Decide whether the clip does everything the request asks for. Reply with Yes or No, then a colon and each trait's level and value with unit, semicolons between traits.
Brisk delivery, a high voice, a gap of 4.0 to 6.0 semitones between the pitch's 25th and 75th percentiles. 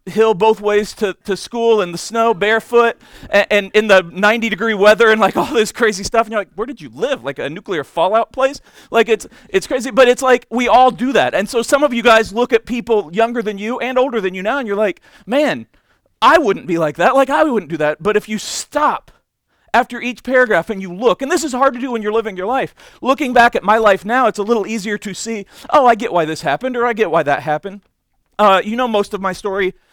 No: fast, 260 wpm; high, 225 Hz; average, 3.2 semitones